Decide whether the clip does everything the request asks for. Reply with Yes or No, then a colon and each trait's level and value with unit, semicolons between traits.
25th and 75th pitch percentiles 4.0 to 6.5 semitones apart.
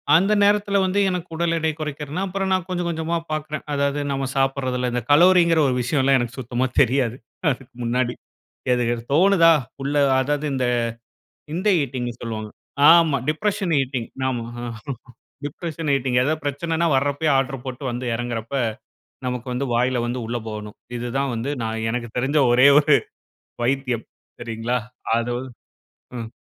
Yes: average, 4.7 semitones